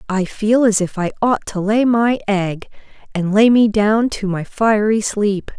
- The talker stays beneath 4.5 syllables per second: Yes, 4.0 syllables/s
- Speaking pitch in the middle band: No, high, 210 Hz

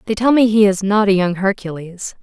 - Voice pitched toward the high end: Yes, high, 200 Hz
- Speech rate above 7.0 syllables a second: No, 5.5 syllables/s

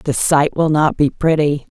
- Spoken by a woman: Yes, female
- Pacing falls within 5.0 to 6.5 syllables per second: No, 4.2 syllables/s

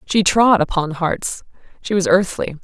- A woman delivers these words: Yes, female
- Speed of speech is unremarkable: Yes, average, 160 wpm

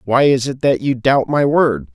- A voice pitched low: Yes, low, 130 Hz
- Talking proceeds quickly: Yes, fast, 245 wpm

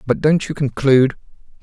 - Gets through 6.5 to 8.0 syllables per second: No, 6.1 syllables/s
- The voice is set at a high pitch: No, medium, 140 Hz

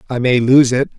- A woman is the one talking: No, male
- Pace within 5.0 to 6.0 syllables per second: Yes, 5.5 syllables/s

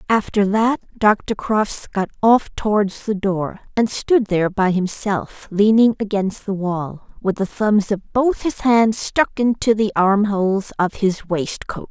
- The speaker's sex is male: No, female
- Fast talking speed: No, average, 160 wpm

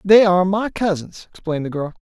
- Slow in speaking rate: No, fast, 205 wpm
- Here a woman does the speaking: No, male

